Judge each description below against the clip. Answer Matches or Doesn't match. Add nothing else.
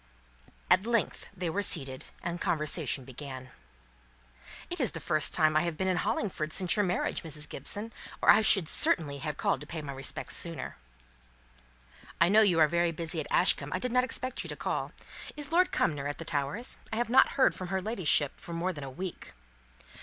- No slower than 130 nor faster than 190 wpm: Doesn't match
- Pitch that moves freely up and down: Doesn't match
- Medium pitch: Matches